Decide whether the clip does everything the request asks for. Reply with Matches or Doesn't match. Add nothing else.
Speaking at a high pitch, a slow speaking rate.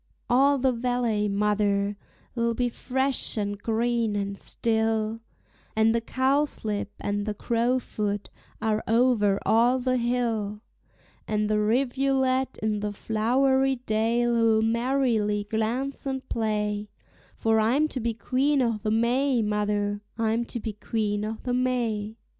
Matches